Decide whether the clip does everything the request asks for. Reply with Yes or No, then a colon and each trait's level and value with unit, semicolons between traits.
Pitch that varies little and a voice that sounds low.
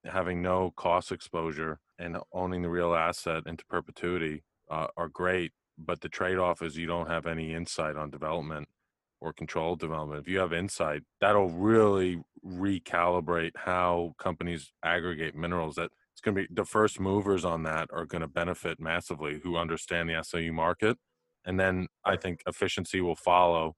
Yes: narrow, 1.9 semitones; very low, 85 Hz